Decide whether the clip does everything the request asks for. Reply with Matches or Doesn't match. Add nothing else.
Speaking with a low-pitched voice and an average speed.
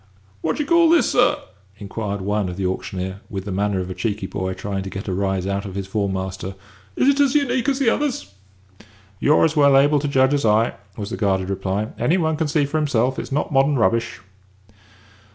Doesn't match